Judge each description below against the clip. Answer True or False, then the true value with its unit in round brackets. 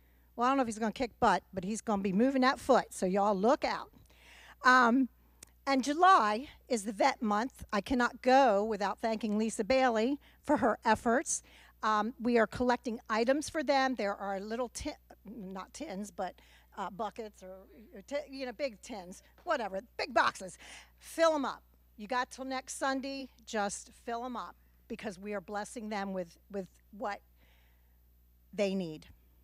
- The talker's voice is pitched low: False (225 Hz)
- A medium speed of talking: True (175 wpm)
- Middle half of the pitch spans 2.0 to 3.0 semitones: False (4.4 semitones)